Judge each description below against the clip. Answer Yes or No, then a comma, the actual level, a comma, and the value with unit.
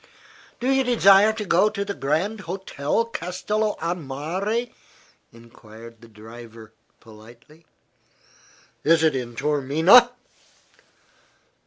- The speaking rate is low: Yes, slow, 105 wpm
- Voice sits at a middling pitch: Yes, medium, 160 Hz